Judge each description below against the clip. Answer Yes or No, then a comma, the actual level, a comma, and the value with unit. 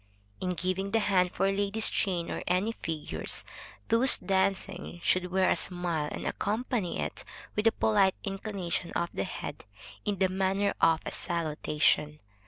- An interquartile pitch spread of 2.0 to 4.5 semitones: Yes, narrow, 2.5 semitones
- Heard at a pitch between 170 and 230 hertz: Yes, high, 190 Hz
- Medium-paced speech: Yes, average, 155 wpm